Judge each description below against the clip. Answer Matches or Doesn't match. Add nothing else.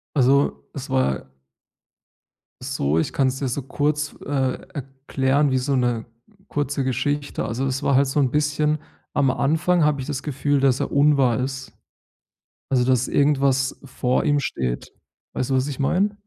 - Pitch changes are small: Matches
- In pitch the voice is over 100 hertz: Matches